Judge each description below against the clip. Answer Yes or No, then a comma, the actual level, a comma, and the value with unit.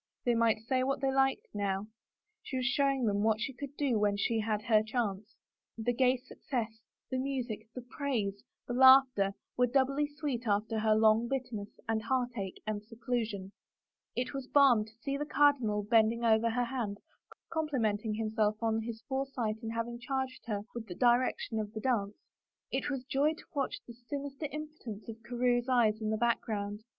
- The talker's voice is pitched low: No, high, 235 Hz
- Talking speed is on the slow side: No, average, 180 wpm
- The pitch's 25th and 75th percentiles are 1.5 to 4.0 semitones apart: Yes, average, 3.4 semitones